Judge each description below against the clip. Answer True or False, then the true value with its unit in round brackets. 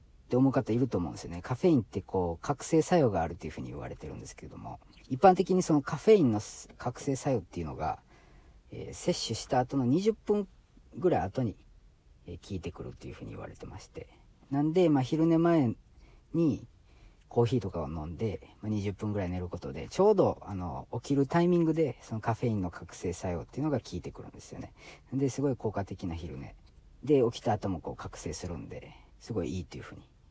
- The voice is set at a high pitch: False (115 Hz)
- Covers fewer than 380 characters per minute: False (420 characters per minute)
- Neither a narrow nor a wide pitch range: False (8.3 semitones)